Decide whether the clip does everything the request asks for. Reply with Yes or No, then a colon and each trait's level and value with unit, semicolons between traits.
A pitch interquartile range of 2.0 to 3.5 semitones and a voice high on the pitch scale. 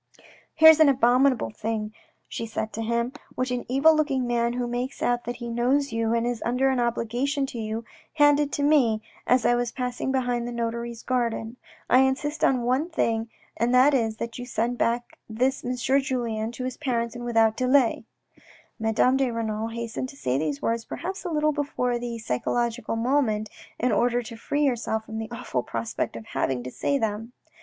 Yes: narrow, 2.5 semitones; high, 240 Hz